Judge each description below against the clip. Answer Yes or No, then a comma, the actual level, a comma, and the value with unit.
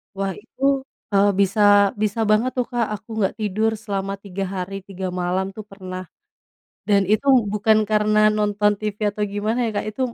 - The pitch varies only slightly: Yes, narrow, 1.6 semitones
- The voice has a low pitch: No, high, 205 Hz